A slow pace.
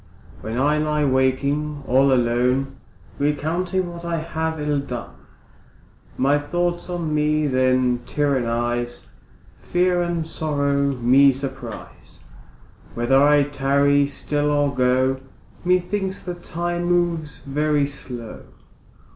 Yes: slow, 110 wpm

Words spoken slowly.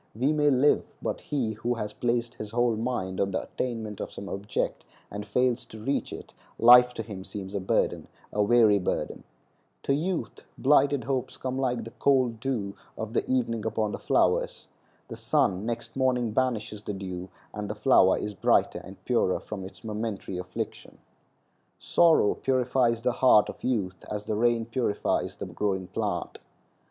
No: average, 165 wpm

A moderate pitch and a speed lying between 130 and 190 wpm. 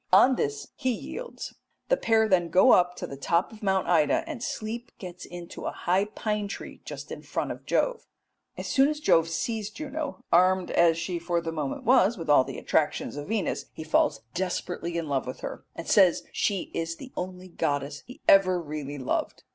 No: medium, 180 Hz; average, 200 wpm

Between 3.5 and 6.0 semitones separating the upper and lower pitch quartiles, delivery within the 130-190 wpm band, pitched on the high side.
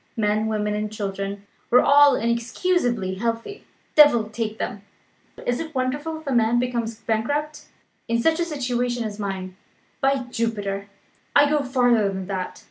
Yes: average, 4.5 semitones; average, 150 wpm; high, 235 Hz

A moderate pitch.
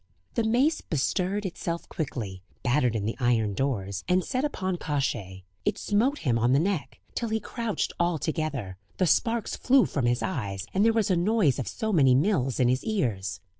Yes: medium, 155 Hz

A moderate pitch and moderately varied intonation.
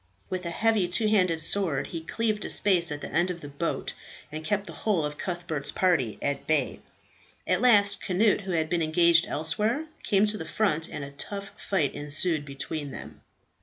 Yes: medium, 175 Hz; average, 4.6 semitones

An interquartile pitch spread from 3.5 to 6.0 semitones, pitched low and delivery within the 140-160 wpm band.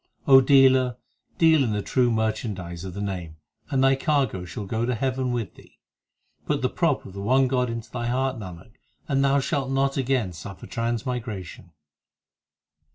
No: average, 4.7 semitones; low, 120 Hz; average, 170 wpm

